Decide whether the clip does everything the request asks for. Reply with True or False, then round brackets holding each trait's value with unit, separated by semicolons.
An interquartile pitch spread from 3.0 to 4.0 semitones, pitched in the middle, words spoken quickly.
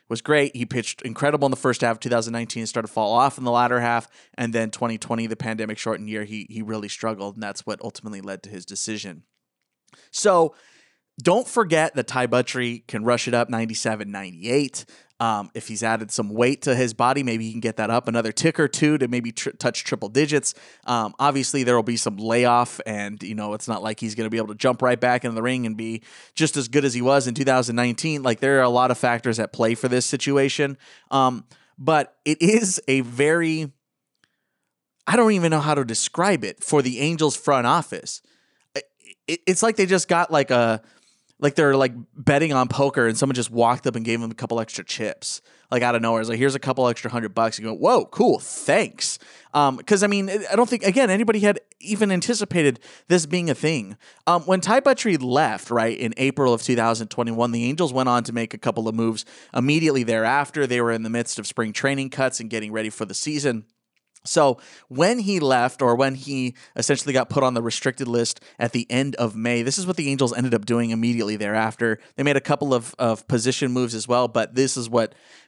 False (3.7 semitones; 125 Hz; 220 wpm)